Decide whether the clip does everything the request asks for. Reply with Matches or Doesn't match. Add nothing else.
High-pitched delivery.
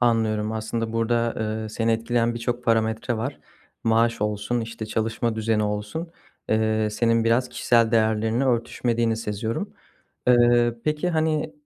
Doesn't match